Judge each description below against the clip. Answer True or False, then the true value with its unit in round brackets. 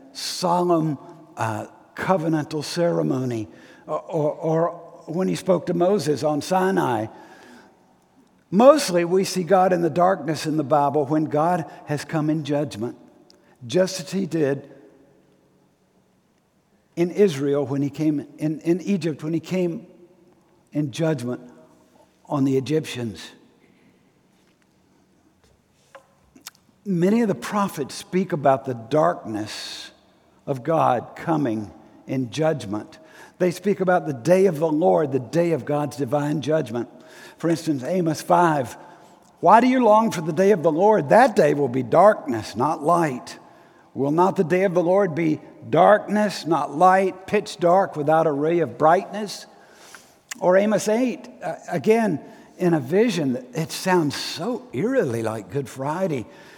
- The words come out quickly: False (140 wpm)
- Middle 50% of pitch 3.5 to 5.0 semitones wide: True (4.0 semitones)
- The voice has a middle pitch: True (165 Hz)